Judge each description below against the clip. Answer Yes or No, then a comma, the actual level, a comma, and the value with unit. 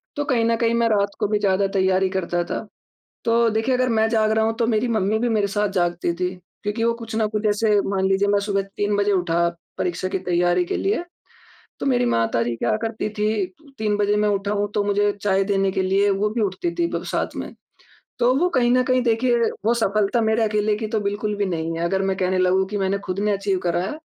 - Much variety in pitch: No, average, 2.8 semitones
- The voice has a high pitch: Yes, high, 205 Hz